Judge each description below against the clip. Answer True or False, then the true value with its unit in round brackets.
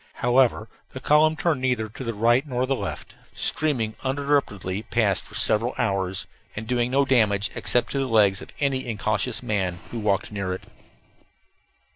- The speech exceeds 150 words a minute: True (165 wpm)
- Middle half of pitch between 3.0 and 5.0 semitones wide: True (4.2 semitones)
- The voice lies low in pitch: True (115 Hz)